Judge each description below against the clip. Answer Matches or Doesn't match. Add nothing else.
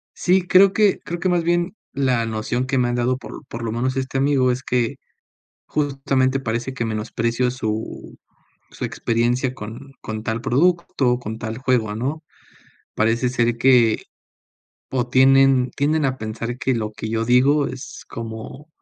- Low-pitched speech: Matches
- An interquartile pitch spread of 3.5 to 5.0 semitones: Doesn't match